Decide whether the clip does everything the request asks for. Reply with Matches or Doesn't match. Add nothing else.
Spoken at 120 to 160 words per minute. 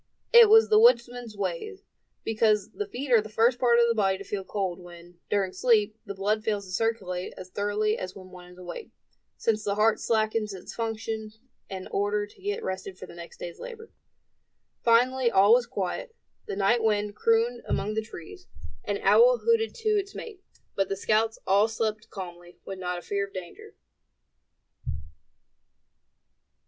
Doesn't match